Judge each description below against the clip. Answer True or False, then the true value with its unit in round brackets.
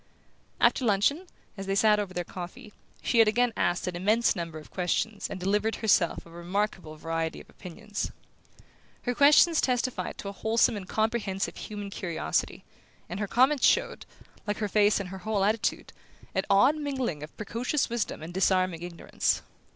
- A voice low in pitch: False (205 Hz)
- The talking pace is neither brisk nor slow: True (170 wpm)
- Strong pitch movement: False (3.9 semitones)